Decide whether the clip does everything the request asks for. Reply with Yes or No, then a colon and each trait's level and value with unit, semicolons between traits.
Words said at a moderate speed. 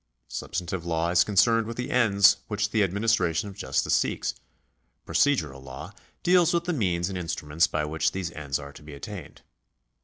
Yes: average, 175 wpm